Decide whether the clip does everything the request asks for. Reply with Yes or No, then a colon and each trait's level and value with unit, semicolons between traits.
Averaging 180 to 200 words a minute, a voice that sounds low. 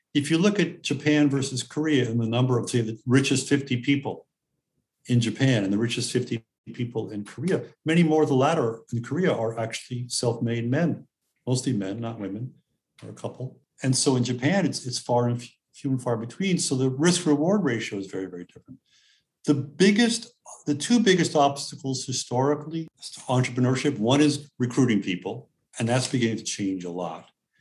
Yes: average, 185 wpm; low, 130 Hz